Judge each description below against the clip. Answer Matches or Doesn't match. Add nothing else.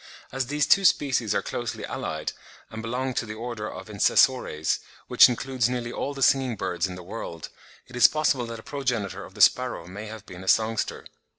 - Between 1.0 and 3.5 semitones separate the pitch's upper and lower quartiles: Doesn't match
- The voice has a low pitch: Matches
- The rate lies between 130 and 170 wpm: Doesn't match